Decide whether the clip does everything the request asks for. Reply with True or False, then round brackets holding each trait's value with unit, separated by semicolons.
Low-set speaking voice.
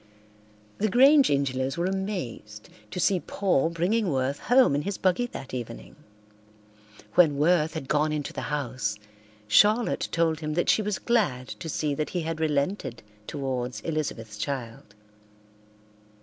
False (155 Hz)